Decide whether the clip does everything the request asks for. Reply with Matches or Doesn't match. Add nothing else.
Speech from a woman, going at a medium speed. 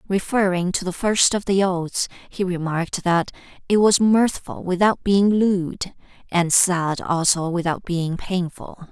Matches